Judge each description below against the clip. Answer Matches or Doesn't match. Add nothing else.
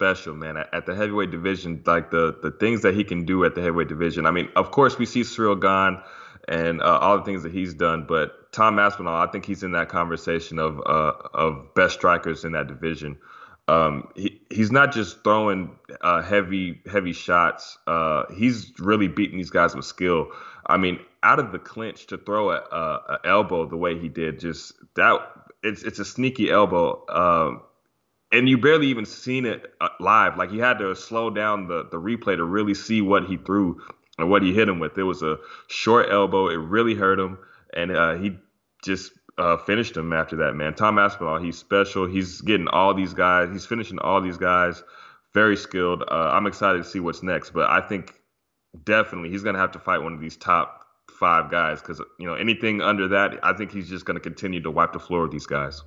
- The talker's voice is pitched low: Matches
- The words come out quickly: Matches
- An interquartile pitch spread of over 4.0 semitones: Doesn't match